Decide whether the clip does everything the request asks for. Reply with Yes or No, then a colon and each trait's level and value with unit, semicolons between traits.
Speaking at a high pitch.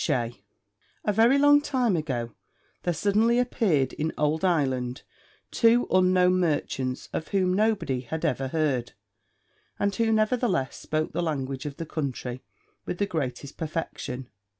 No: medium, 165 Hz